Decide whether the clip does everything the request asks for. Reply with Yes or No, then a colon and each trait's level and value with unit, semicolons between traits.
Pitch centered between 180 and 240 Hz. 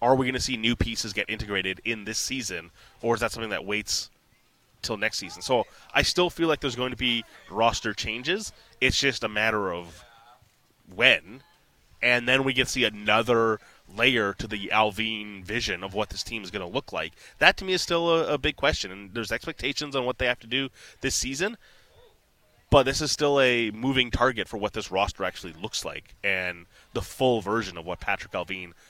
No: low, 115 Hz